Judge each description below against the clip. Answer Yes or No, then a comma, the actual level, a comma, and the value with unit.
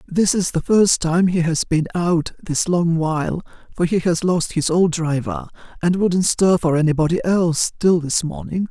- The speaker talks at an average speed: Yes, average, 195 wpm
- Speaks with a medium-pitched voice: Yes, medium, 170 Hz